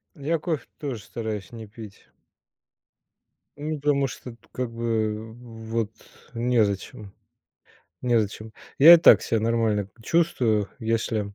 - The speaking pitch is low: Yes, low, 115 Hz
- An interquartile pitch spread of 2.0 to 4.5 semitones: Yes, average, 2.9 semitones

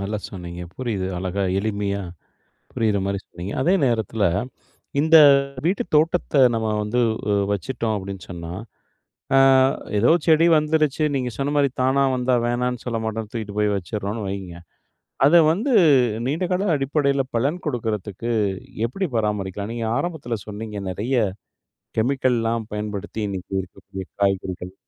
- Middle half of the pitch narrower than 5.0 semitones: No, average, 5.3 semitones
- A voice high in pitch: No, low, 110 Hz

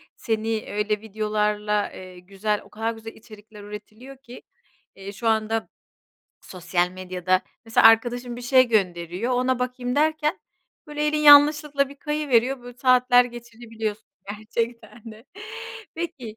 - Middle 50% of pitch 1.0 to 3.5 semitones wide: Yes, average, 3.2 semitones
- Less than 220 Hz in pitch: No, high, 225 Hz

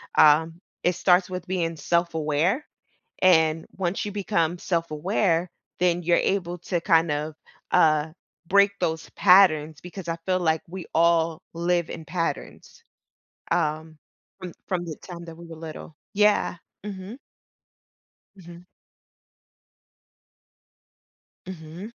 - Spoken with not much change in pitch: Yes, narrow, 2.2 semitones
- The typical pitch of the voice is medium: Yes, medium, 170 Hz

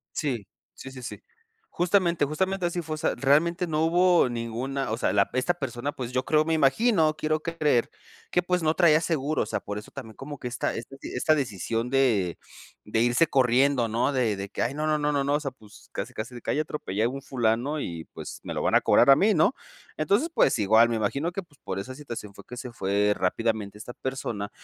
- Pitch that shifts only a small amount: No, average, 5.2 semitones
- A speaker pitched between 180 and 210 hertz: No, low, 135 Hz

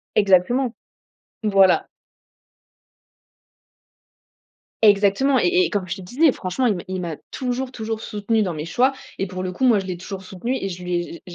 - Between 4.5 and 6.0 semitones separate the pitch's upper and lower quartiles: Yes, average, 5.0 semitones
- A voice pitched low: No, high, 200 Hz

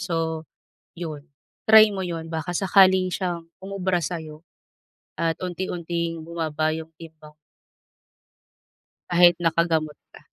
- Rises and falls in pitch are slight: Yes, narrow, 2.0 semitones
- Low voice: No, medium, 170 Hz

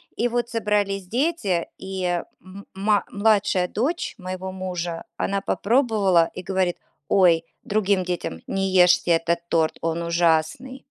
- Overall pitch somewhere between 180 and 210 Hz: Yes, high, 190 Hz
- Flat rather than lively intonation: No, average, 3.0 semitones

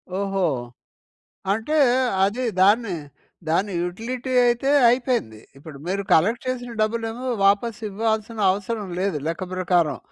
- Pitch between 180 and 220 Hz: Yes, high, 210 Hz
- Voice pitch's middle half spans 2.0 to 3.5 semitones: No, average, 4.1 semitones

